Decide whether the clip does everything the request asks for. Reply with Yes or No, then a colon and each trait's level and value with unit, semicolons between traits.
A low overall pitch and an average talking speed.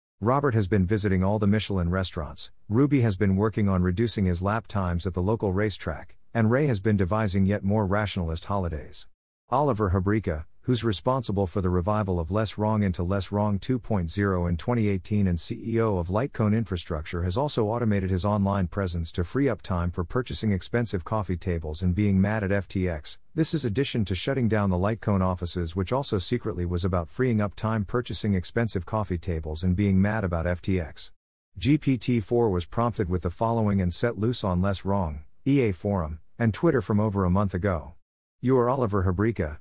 Yes: low, 100 Hz; average, 185 wpm